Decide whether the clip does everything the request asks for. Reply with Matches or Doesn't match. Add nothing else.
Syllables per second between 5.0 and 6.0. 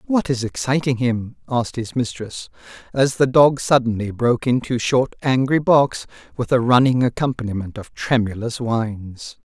Doesn't match